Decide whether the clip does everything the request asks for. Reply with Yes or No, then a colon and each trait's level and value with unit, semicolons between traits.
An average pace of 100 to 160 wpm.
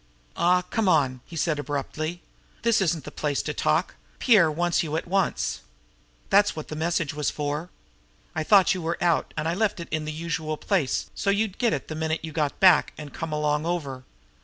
No: fast, 205 wpm